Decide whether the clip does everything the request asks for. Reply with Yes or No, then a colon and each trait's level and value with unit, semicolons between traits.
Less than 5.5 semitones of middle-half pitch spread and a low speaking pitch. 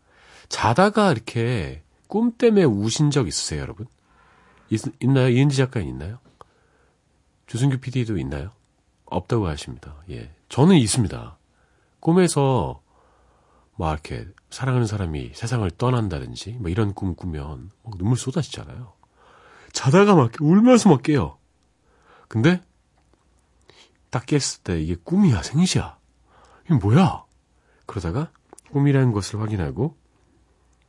No: wide, 7.4 semitones; low, 120 Hz